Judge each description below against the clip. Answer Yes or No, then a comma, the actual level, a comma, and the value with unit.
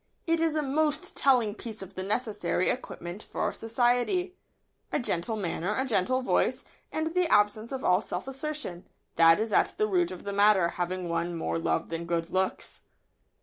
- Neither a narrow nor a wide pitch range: No, wide, 6.8 semitones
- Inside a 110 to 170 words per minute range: No, average, 180 wpm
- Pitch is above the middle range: Yes, high, 210 Hz